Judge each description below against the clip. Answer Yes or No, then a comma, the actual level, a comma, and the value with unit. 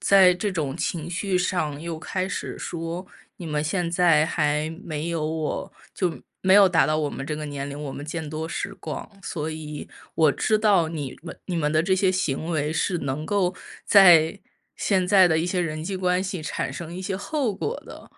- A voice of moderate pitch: Yes, medium, 165 Hz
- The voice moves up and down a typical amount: Yes, average, 3.3 semitones